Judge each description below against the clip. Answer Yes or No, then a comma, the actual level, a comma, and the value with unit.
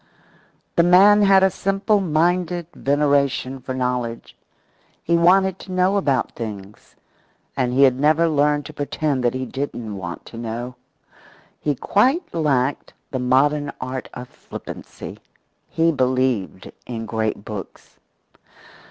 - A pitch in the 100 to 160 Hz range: Yes, medium, 140 Hz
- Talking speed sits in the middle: No, slow, 130 wpm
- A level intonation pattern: No, average, 5.3 semitones